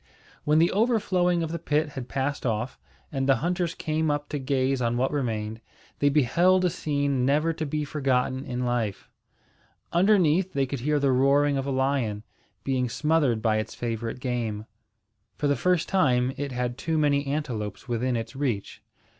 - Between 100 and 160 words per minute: No, average, 175 wpm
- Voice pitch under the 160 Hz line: Yes, medium, 140 Hz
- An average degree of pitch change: Yes, average, 3.7 semitones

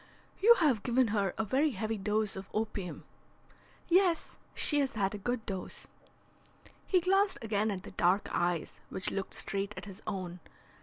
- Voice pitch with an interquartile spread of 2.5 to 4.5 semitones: No, average, 5.3 semitones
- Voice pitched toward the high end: Yes, high, 215 Hz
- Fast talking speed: No, average, 165 wpm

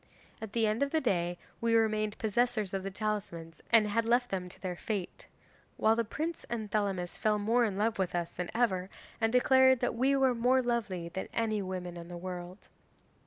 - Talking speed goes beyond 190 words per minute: Yes, fast, 205 wpm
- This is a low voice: No, high, 215 Hz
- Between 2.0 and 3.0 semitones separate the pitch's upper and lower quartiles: No, average, 4.1 semitones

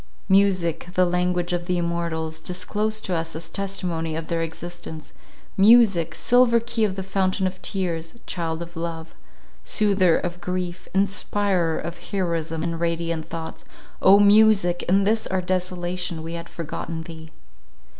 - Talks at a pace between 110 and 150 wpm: Yes, average, 140 wpm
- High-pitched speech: No, medium, 175 Hz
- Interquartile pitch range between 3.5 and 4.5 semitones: No, narrow, 2.6 semitones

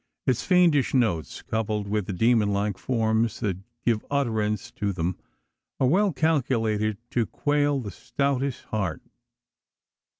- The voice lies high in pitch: No, low, 110 Hz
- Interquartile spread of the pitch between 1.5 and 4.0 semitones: No, average, 4.7 semitones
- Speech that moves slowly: Yes, slow, 130 wpm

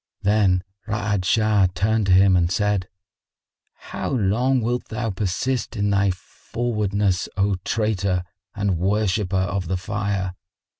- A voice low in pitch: Yes, low, 100 Hz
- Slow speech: Yes, slow, 130 wpm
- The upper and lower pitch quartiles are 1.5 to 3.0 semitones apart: Yes, narrow, 2.4 semitones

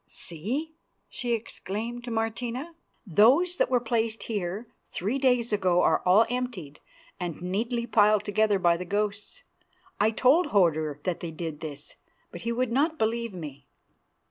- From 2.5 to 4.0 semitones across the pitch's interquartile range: No, average, 5.1 semitones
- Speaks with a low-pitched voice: No, high, 215 Hz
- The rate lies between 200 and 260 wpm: No, average, 150 wpm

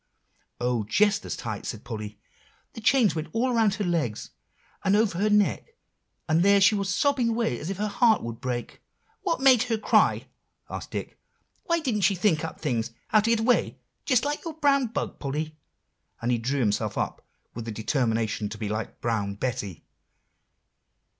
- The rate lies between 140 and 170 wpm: No, average, 180 wpm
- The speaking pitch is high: No, medium, 180 Hz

